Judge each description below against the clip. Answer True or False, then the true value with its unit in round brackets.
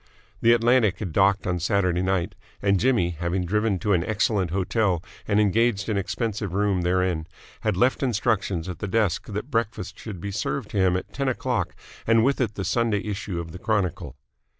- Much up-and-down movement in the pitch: False (3.6 semitones)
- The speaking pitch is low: True (100 Hz)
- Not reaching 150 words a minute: False (190 wpm)